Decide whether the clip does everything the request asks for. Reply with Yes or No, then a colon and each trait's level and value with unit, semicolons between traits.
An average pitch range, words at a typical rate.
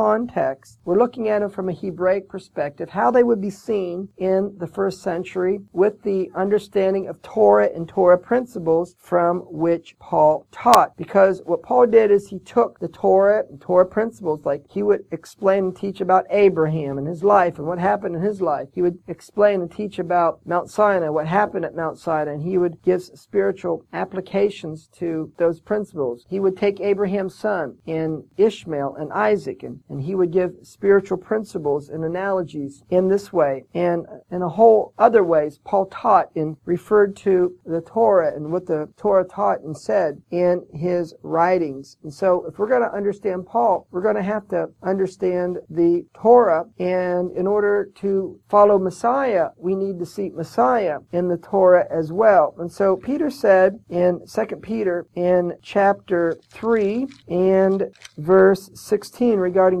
Yes: average, 3.0 semitones; average, 170 wpm